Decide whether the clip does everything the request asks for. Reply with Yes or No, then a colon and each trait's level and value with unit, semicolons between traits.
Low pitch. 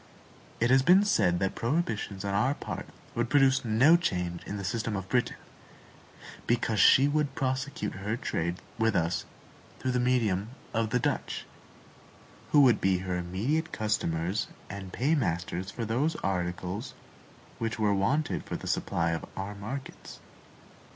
Yes: low, 110 Hz